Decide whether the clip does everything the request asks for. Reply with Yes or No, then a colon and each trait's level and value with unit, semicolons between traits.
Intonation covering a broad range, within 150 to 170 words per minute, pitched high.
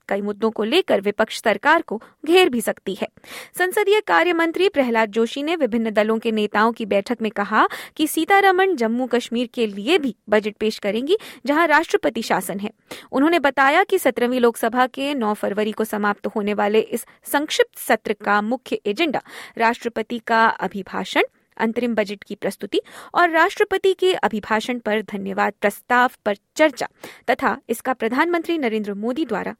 Yes: wide, 6.4 semitones; average, 160 wpm; high, 235 Hz